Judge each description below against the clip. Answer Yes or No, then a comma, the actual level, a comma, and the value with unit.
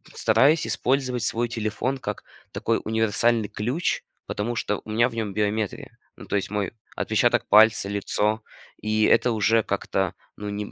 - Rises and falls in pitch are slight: Yes, narrow, 2.2 semitones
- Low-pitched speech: Yes, low, 110 Hz